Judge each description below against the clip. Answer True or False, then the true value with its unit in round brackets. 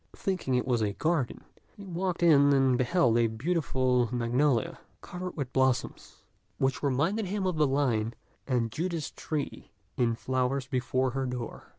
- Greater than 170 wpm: False (155 wpm)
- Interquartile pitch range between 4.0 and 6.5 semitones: True (4.8 semitones)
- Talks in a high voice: False (135 Hz)